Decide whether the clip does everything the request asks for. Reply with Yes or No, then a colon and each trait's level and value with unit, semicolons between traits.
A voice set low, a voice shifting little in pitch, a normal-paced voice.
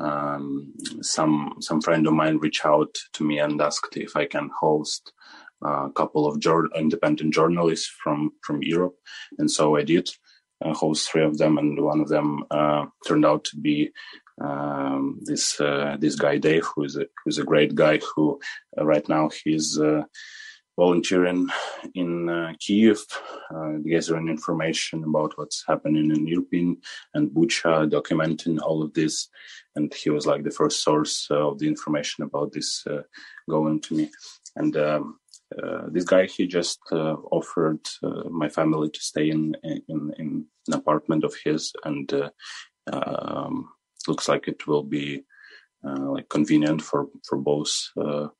Yes: very low, 75 Hz; narrow, 1.5 semitones; average, 165 wpm